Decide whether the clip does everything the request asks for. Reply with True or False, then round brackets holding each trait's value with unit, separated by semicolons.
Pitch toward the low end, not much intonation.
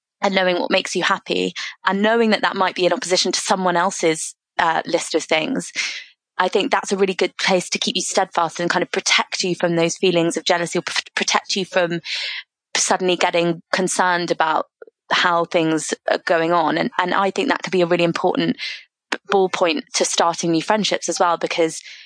False (180 Hz; 2.1 semitones)